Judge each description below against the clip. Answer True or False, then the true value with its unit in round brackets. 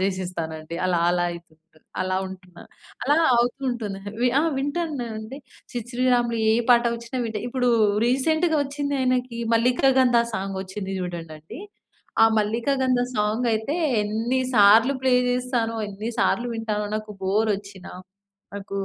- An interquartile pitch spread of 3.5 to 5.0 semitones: True (4.4 semitones)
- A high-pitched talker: True (225 Hz)